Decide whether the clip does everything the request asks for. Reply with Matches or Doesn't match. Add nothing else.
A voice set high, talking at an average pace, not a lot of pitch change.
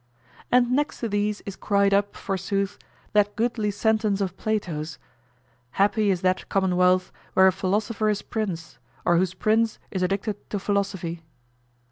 Matches